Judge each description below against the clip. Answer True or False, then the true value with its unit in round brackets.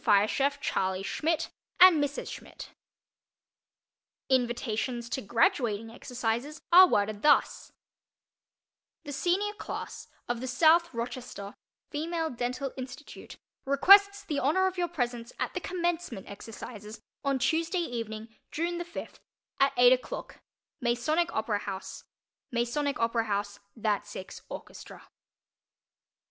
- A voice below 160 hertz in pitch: False (255 Hz)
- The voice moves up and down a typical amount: False (6.2 semitones)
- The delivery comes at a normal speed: False (110 wpm)